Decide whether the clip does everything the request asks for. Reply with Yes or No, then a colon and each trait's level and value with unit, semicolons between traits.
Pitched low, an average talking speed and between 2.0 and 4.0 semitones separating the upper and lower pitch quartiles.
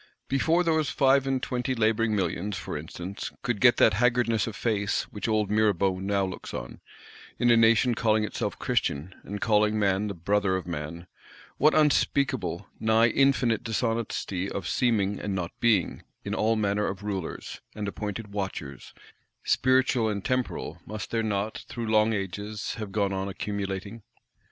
Yes: low, 105 Hz; average, 155 wpm; average, 3.0 semitones